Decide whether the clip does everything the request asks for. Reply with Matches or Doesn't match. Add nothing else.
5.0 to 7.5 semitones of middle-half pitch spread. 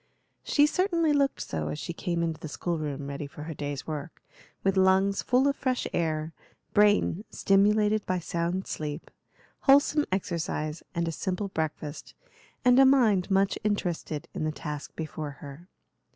Matches